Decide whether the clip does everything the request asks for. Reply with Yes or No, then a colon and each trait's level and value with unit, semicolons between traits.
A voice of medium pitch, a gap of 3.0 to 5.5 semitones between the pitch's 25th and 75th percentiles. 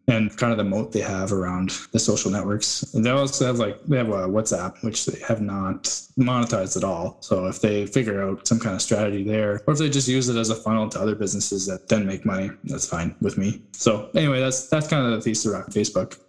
No: low, 110 Hz; average, 3.5 semitones